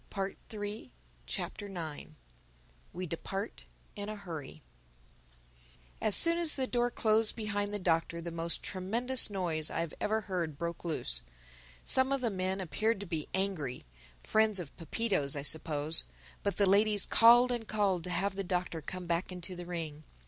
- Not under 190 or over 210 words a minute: No, average, 165 wpm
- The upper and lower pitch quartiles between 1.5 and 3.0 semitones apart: No, average, 4.2 semitones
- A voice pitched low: No, high, 190 Hz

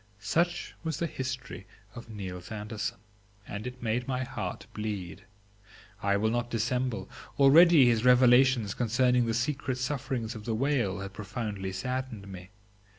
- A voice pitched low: Yes, low, 120 Hz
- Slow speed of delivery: No, average, 145 wpm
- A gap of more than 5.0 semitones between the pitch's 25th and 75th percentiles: No, average, 3.6 semitones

